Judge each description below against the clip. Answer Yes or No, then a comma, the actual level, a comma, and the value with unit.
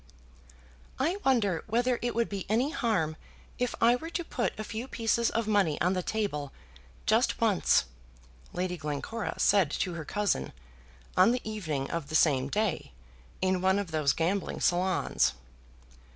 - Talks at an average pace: Yes, average, 155 wpm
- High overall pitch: Yes, high, 200 Hz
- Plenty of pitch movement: Yes, wide, 5.8 semitones